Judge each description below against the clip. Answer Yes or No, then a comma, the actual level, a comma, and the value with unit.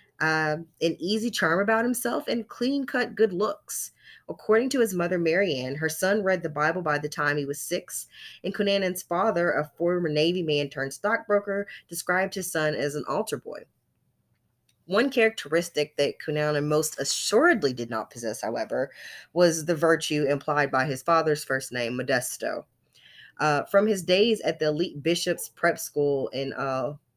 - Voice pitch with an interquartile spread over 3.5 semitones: Yes, average, 4.8 semitones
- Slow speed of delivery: No, average, 165 wpm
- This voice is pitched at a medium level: Yes, medium, 165 Hz